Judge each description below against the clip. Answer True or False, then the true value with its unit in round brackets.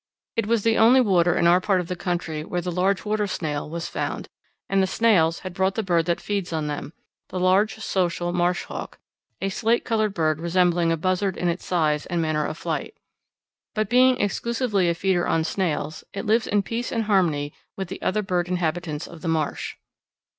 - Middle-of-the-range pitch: True (180 Hz)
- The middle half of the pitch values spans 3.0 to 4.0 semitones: True (3.4 semitones)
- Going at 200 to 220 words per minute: True (205 wpm)